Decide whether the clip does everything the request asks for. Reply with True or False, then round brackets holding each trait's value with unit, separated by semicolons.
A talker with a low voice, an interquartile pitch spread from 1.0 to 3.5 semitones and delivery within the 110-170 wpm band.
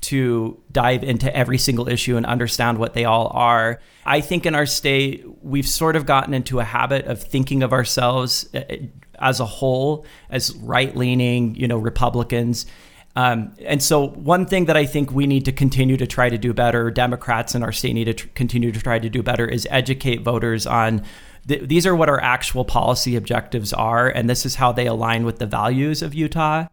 False (125 Hz; 2.6 semitones; 200 wpm)